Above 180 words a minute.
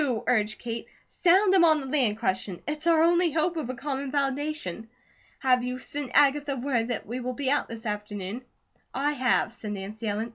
Yes: average, 190 wpm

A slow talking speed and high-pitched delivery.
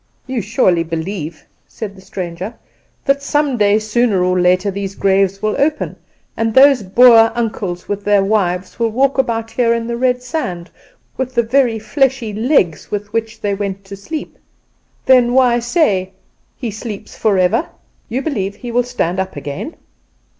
No: average, 160 wpm; high, 215 Hz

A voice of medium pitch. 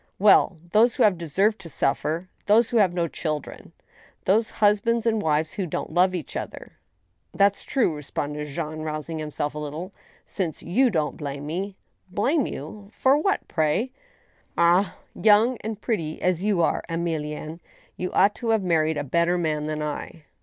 Yes: medium, 175 Hz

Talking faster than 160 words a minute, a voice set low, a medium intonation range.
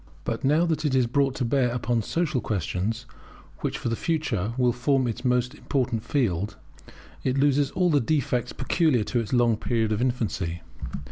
Yes: average, 180 wpm; low, 125 Hz; average, 3.5 semitones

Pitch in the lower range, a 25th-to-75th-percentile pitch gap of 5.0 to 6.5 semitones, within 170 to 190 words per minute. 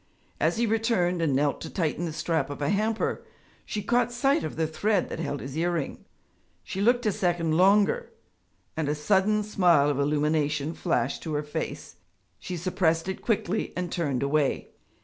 No: medium, 170 Hz; wide, 5.4 semitones; average, 175 wpm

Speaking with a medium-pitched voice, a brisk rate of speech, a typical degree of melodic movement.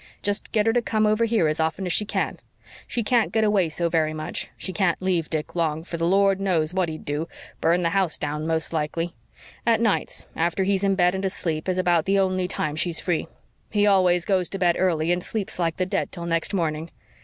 Yes: medium, 180 Hz; fast, 230 wpm; average, 3.2 semitones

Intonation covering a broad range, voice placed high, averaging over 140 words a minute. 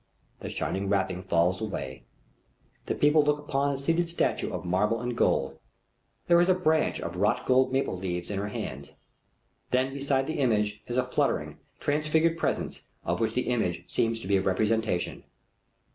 No: wide, 7.1 semitones; low, 115 Hz; average, 175 wpm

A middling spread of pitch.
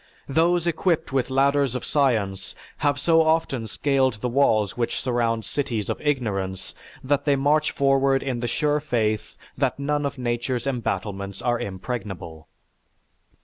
Yes: average, 4.2 semitones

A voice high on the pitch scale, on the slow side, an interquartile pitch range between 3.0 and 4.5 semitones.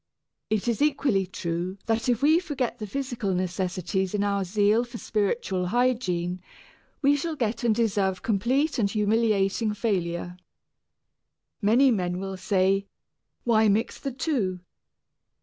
Yes: high, 210 Hz; slow, 130 wpm; average, 4.2 semitones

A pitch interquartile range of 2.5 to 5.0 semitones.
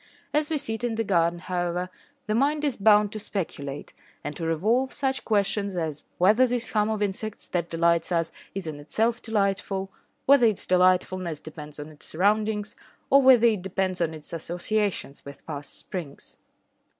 Yes: average, 4.6 semitones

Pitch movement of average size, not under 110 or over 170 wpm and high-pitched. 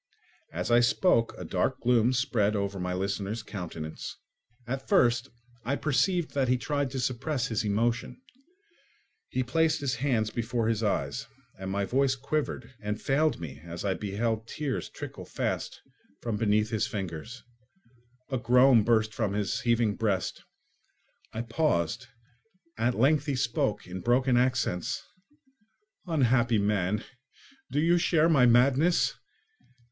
No: average, 4.2 semitones; average, 140 wpm; low, 120 Hz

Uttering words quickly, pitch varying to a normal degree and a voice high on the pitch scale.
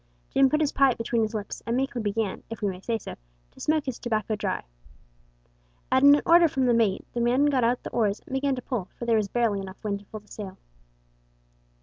Yes: fast, 235 wpm; average, 4.1 semitones; high, 235 Hz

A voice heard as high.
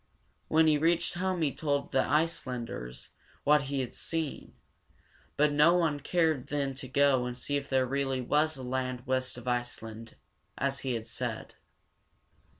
No: medium, 140 Hz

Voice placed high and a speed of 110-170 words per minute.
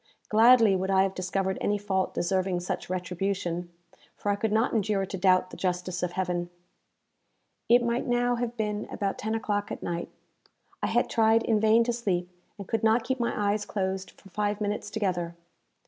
No: high, 200 Hz; average, 185 wpm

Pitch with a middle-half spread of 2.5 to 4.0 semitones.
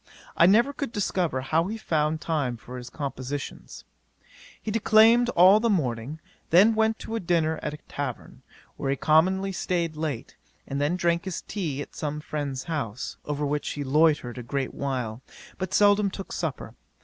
No: wide, 5.4 semitones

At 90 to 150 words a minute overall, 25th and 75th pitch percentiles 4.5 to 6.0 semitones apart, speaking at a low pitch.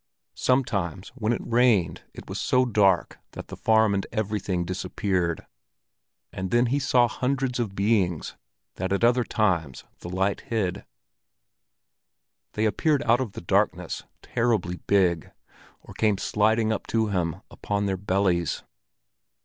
No: average, 140 wpm; average, 3.9 semitones; low, 105 Hz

